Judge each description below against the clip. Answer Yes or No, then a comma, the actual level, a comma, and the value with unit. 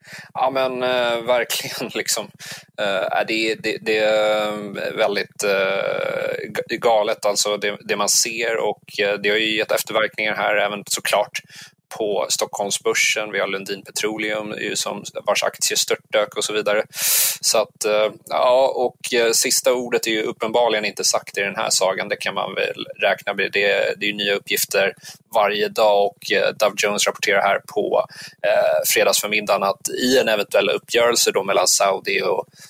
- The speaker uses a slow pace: No, average, 155 wpm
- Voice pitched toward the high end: No, low, 110 Hz